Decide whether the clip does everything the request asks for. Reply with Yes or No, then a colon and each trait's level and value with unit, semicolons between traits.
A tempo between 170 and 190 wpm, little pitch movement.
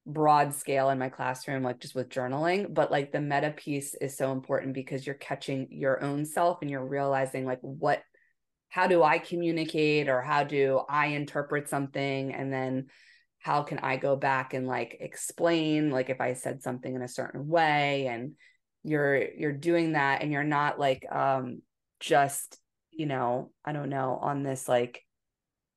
Yes: average, 175 wpm; narrow, 2.1 semitones